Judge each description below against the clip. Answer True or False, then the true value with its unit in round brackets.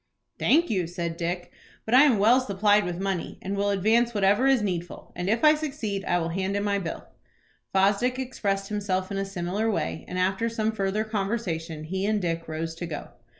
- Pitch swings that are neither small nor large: True (3.6 semitones)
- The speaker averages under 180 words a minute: False (200 wpm)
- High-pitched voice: True (195 Hz)